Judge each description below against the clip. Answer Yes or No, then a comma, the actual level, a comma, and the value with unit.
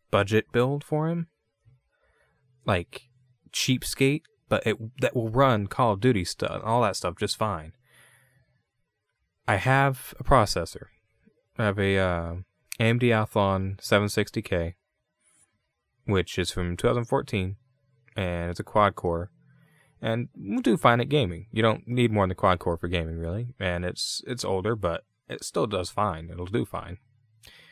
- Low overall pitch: Yes, low, 110 Hz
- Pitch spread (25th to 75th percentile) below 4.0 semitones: No, average, 5.1 semitones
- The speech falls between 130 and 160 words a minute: Yes, average, 150 wpm